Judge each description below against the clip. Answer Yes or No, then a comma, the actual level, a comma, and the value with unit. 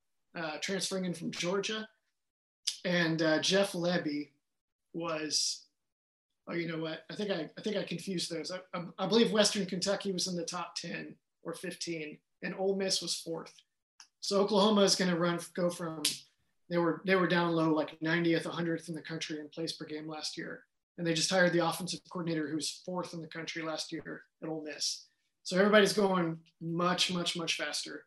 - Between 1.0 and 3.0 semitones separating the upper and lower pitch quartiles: Yes, narrow, 2.5 semitones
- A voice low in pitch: No, medium, 170 Hz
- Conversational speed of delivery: Yes, average, 190 wpm